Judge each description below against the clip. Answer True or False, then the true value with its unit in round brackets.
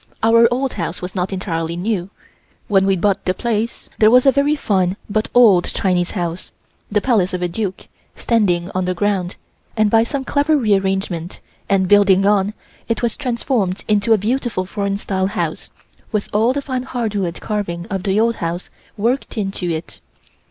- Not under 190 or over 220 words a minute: False (180 wpm)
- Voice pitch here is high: True (200 Hz)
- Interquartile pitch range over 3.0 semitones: True (3.8 semitones)